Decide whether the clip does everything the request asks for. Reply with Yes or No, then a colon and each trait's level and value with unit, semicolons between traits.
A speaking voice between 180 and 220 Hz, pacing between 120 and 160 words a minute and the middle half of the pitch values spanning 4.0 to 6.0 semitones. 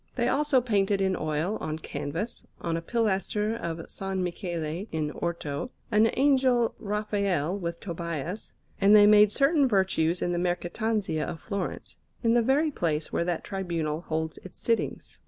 Yes: high, 190 Hz; average, 155 wpm; average, 4.7 semitones